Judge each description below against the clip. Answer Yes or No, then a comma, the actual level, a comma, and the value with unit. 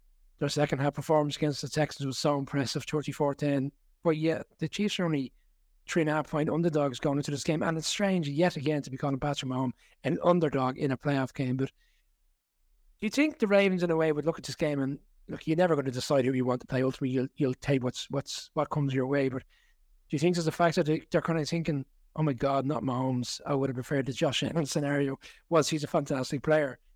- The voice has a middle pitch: Yes, medium, 145 Hz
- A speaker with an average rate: No, fast, 245 wpm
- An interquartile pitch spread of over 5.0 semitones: No, average, 3.0 semitones